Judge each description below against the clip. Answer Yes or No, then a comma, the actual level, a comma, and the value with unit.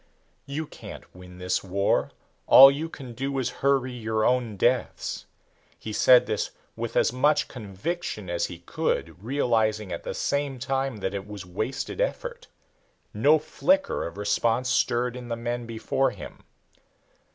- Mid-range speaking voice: No, low, 120 Hz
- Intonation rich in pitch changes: No, average, 4.7 semitones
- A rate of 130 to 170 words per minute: Yes, average, 150 wpm